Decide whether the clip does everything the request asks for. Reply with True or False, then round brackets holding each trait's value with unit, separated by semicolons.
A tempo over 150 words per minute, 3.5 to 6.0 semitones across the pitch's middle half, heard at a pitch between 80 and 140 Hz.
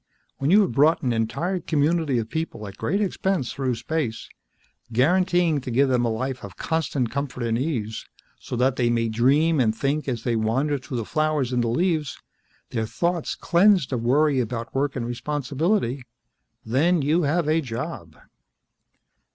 True (170 wpm; 5.1 semitones; 135 Hz)